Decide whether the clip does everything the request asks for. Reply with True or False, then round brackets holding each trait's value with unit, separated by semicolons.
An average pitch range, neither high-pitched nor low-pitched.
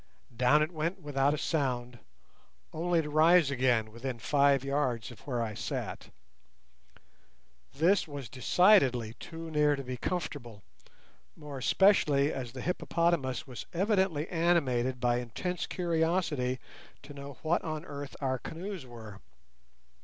True (4.8 semitones; 145 Hz)